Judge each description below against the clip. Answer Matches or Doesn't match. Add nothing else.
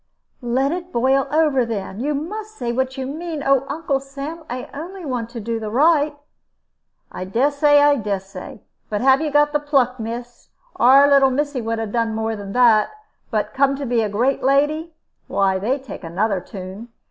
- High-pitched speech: Matches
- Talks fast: Doesn't match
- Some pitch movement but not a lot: Matches